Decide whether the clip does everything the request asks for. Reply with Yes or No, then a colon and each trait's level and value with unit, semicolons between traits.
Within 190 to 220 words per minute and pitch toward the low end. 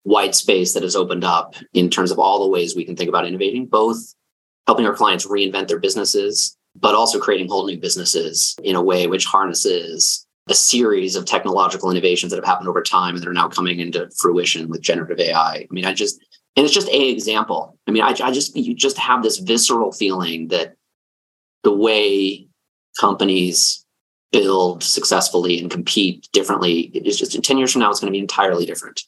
Yes: average, 200 wpm; low, 110 Hz